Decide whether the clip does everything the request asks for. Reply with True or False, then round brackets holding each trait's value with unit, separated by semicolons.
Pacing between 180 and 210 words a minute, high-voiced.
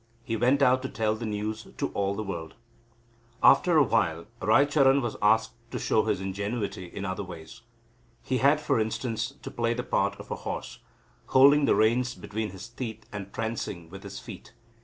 False (185 wpm; 110 Hz)